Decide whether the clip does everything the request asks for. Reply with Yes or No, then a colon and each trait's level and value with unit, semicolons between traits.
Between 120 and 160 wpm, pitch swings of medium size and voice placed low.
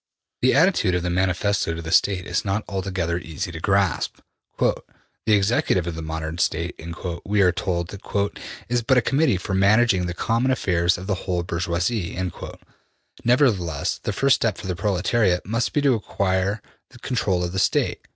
No: average, 170 wpm; average, 3.6 semitones; very low, 95 Hz